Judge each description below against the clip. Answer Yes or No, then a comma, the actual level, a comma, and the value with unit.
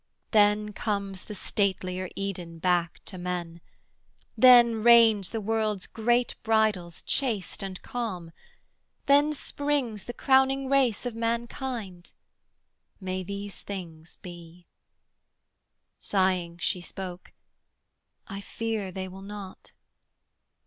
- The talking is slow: Yes, slow, 105 wpm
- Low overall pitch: No, high, 200 Hz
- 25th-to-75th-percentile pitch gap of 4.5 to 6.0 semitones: No, average, 4.0 semitones